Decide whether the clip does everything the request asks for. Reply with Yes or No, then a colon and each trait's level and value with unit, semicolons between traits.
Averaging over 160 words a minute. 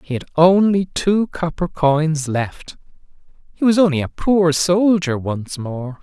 No: average, 150 wpm